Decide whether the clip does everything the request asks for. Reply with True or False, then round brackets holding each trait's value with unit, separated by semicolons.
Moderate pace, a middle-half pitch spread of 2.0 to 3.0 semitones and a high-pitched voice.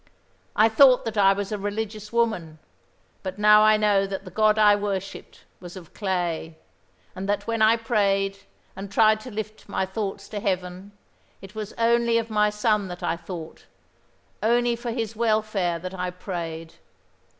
True (170 wpm; 2.5 semitones; 205 Hz)